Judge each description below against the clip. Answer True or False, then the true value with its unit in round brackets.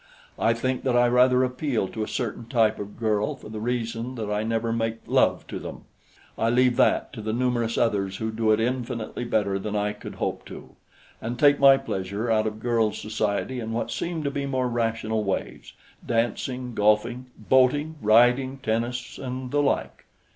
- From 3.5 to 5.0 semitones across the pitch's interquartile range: False (2.6 semitones)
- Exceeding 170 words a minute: True (185 wpm)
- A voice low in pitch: True (115 Hz)